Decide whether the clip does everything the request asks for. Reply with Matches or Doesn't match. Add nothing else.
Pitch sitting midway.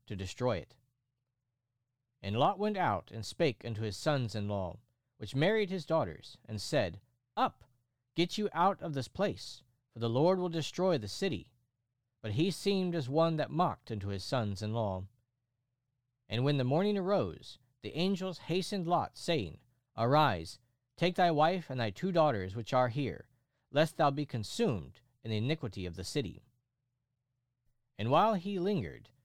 Doesn't match